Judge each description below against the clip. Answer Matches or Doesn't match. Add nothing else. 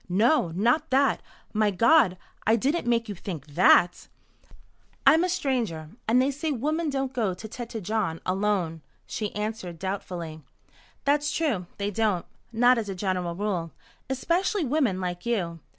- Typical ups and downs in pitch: Doesn't match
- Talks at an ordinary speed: Matches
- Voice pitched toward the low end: Doesn't match